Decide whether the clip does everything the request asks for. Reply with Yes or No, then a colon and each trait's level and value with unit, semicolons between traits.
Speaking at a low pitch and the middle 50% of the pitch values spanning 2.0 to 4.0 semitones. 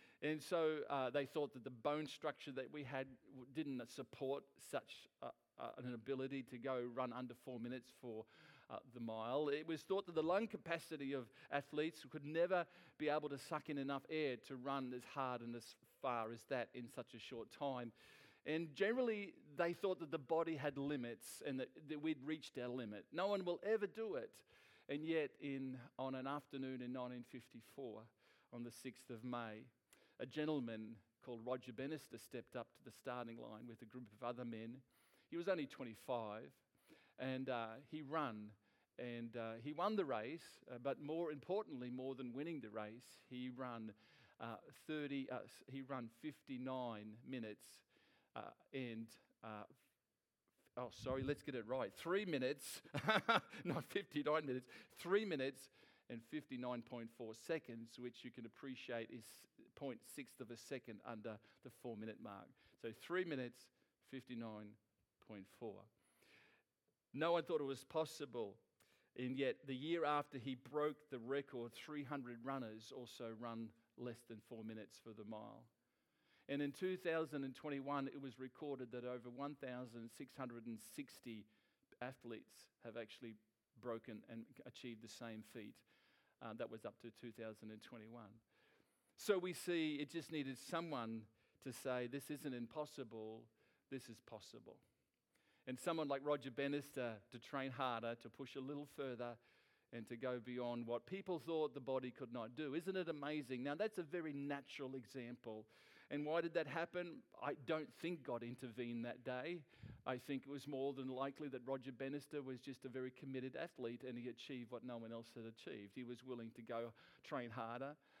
Yes: low, 130 Hz; average, 3.7 semitones